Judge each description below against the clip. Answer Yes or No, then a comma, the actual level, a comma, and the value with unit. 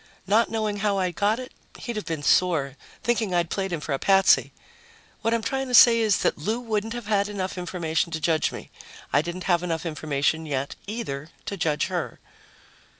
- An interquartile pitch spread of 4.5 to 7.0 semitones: Yes, average, 5.2 semitones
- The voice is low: No, high, 190 Hz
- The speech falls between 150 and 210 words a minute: Yes, average, 200 wpm